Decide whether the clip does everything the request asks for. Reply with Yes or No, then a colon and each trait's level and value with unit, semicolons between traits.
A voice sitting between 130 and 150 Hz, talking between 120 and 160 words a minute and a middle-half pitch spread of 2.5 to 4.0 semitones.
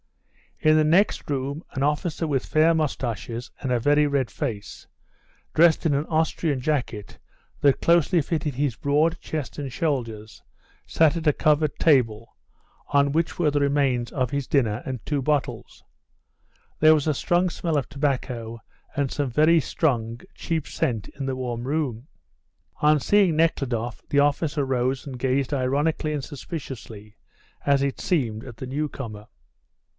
Yes: medium, 140 Hz; average, 155 wpm; average, 3.6 semitones